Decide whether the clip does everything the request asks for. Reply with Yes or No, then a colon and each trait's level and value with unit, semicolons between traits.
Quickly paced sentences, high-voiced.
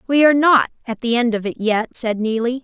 Yes: fast, 250 wpm; high, 240 Hz